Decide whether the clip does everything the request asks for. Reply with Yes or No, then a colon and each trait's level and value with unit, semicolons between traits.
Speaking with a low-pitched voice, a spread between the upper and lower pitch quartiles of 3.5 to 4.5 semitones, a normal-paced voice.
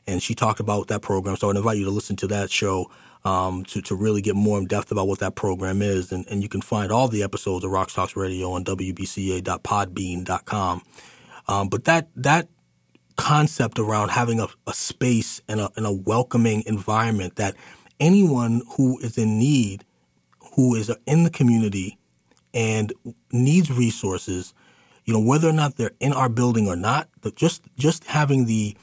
Yes: low, 105 Hz; average, 4.2 semitones; average, 180 wpm